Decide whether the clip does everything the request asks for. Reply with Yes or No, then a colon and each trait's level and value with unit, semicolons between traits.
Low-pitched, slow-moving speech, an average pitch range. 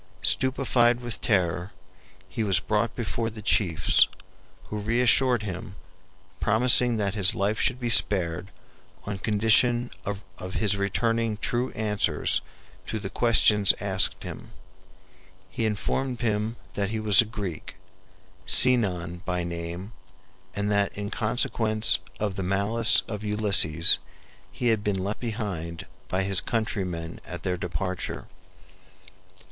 Yes: low, 105 Hz; slow, 125 wpm; average, 3.3 semitones